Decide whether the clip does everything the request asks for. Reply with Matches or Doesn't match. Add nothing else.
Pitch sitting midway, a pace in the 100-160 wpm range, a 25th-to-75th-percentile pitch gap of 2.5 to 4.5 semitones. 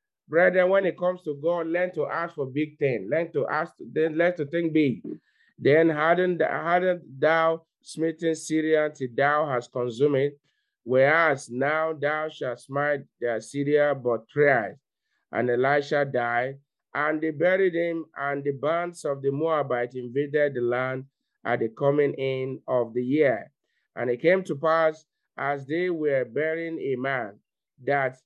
Matches